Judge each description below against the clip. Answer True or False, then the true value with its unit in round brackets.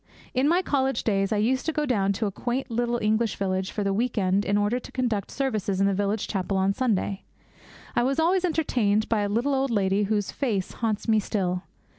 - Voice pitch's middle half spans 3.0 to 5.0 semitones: True (4.3 semitones)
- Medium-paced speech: False (220 wpm)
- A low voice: False (215 Hz)